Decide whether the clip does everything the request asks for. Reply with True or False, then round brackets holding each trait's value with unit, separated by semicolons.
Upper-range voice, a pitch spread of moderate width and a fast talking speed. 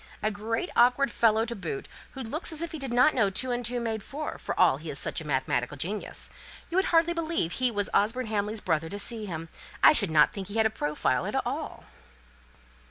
False (220 Hz; 5.7 semitones; 230 wpm)